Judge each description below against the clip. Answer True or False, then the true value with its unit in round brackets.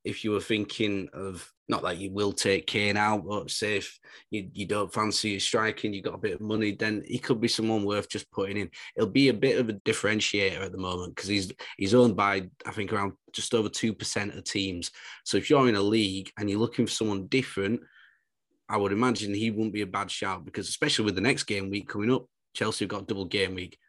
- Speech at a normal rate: False (245 wpm)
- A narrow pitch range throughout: True (2.0 semitones)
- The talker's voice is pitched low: True (105 Hz)